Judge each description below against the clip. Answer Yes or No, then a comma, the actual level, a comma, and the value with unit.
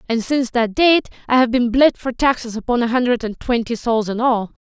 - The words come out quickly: Yes, fast, 235 wpm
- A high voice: Yes, high, 240 Hz